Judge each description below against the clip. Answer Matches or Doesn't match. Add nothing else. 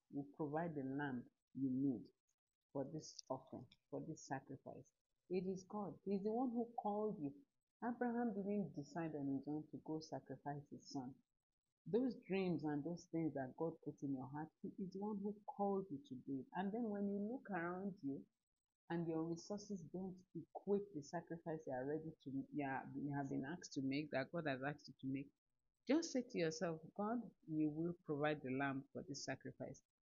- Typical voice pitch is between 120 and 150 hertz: Doesn't match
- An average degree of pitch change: Doesn't match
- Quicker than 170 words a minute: Matches